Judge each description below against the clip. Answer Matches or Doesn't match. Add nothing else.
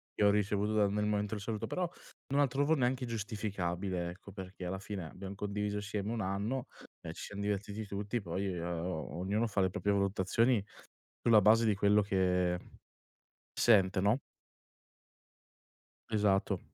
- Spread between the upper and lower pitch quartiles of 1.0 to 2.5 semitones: Matches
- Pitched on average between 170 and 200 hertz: Doesn't match